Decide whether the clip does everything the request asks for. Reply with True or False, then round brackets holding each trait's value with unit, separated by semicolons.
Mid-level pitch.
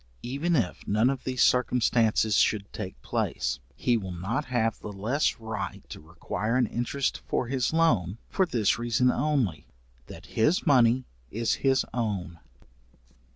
False (115 Hz)